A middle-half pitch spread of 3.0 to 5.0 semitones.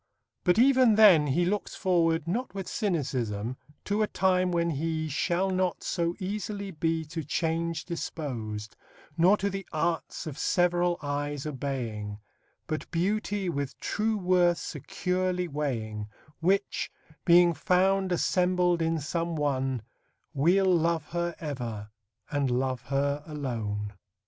Yes: average, 4.4 semitones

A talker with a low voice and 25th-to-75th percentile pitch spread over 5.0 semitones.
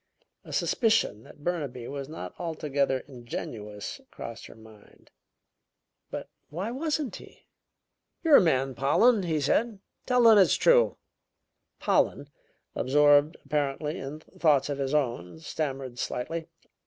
No: medium, 150 Hz; wide, 5.4 semitones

